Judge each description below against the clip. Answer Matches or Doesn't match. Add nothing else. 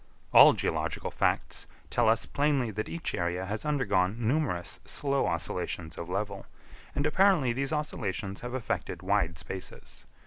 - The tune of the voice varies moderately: Doesn't match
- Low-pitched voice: Matches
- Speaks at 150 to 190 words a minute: Doesn't match